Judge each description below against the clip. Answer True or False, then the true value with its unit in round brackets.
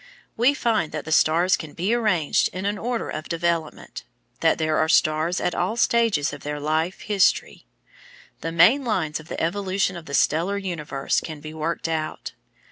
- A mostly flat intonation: False (4.2 semitones)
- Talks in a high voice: False (170 Hz)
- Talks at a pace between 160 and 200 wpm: True (180 wpm)